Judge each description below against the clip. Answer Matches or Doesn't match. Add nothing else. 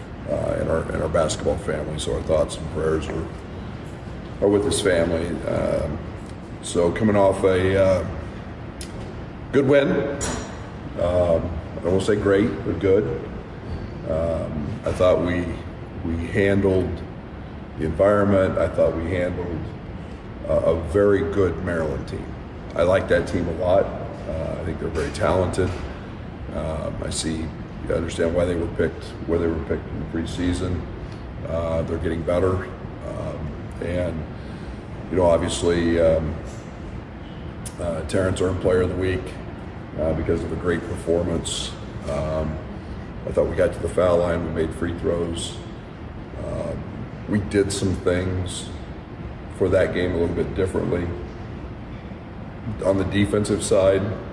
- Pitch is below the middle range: Matches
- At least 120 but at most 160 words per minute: Matches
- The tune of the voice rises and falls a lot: Doesn't match